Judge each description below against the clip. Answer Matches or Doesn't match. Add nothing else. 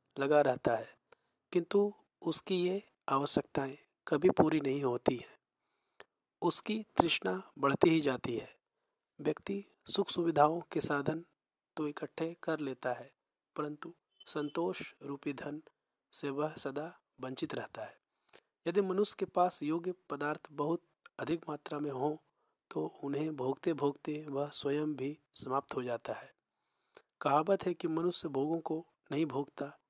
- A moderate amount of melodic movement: Matches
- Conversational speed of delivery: Matches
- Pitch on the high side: Doesn't match